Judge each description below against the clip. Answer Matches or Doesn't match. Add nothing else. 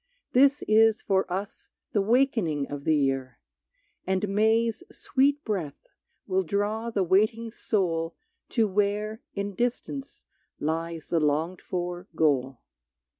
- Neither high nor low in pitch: Doesn't match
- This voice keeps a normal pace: Doesn't match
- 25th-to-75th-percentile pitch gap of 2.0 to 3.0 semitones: Doesn't match